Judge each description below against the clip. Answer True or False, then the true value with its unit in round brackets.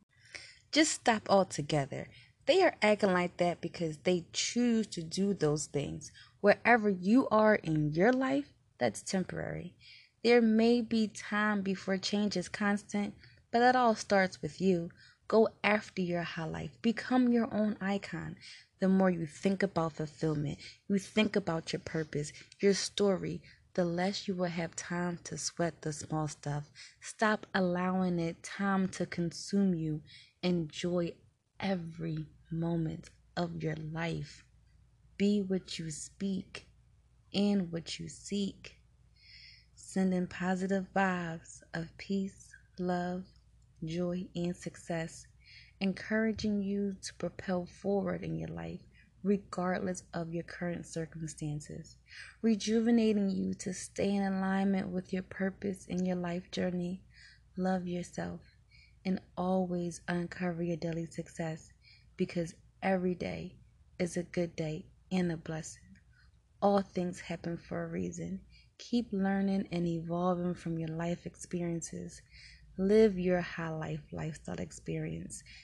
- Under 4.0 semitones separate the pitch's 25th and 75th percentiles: True (3.2 semitones)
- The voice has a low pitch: False (180 Hz)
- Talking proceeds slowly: True (130 wpm)